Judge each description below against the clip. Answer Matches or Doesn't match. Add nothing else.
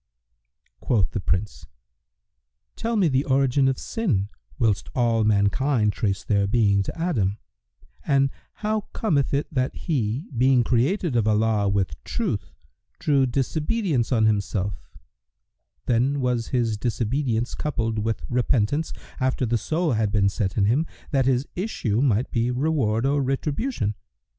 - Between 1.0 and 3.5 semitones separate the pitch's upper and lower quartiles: Doesn't match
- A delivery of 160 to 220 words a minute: Doesn't match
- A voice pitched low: Matches